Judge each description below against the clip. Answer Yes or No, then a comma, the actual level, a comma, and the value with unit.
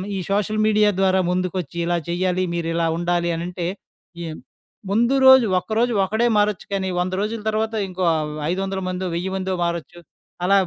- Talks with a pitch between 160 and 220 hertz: Yes, high, 190 Hz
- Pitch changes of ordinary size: Yes, average, 3.2 semitones